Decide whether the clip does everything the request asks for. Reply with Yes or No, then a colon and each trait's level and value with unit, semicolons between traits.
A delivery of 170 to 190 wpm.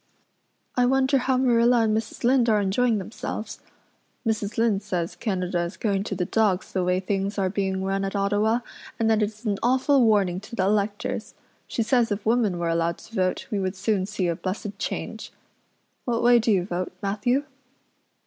Yes: average, 185 wpm